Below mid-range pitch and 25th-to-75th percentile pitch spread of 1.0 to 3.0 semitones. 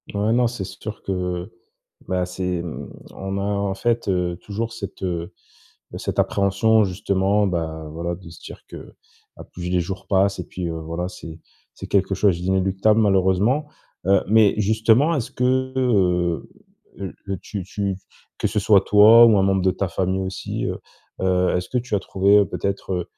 Yes: very low, 95 Hz; narrow, 2.5 semitones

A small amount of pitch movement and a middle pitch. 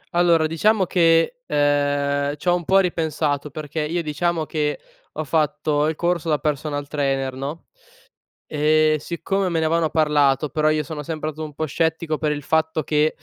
Yes: narrow, 1.9 semitones; medium, 155 Hz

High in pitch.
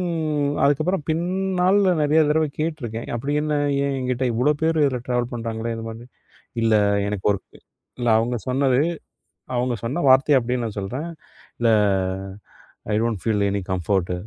No: low, 125 Hz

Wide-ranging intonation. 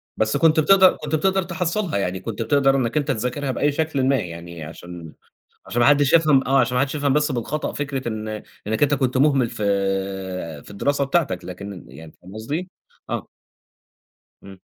Yes: wide, 5.7 semitones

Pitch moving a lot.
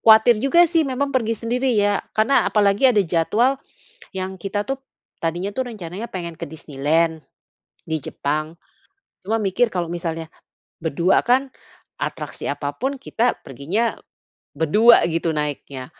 Yes: wide, 6.4 semitones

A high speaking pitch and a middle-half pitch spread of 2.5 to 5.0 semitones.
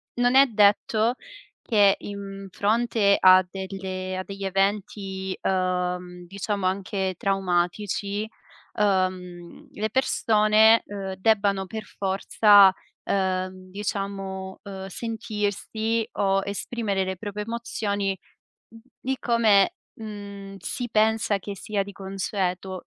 No: high, 200 Hz; narrow, 2.0 semitones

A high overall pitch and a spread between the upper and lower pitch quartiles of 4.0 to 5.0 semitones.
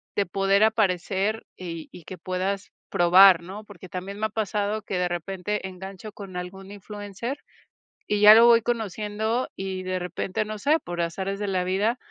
No: high, 195 Hz; narrow, 2.4 semitones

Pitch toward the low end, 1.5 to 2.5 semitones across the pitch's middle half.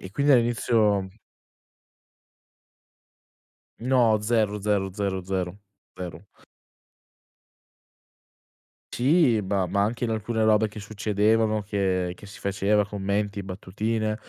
Yes: low, 105 Hz; narrow, 2.2 semitones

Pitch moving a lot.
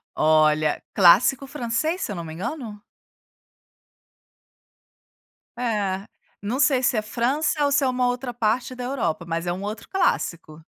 Yes: wide, 6.5 semitones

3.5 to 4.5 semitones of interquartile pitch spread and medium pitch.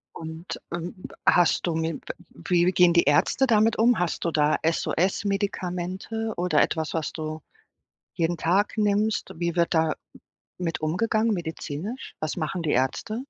Yes: average, 4.0 semitones; medium, 175 Hz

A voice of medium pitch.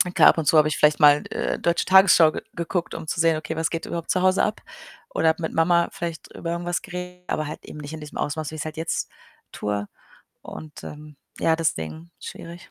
Yes: medium, 160 Hz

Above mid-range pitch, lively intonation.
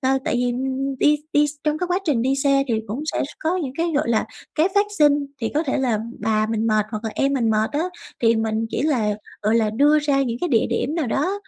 No: very high, 270 Hz; average, 4.9 semitones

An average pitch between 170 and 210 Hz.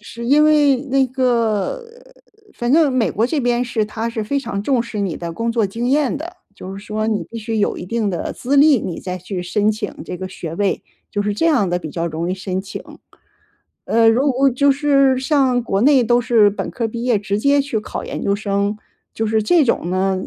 No: high, 230 Hz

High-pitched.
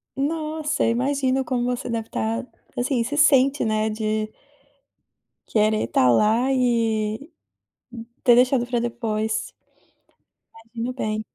Yes: high, 240 Hz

